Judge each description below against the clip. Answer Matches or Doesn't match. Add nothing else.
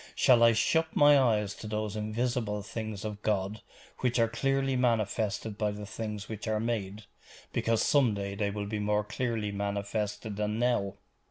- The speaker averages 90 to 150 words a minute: Doesn't match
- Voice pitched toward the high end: Doesn't match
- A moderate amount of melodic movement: Doesn't match